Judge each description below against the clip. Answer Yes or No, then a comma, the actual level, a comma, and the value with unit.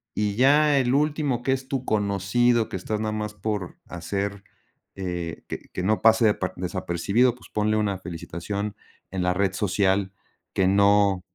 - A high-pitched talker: No, low, 100 Hz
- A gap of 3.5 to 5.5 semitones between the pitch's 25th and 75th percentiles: No, average, 3.1 semitones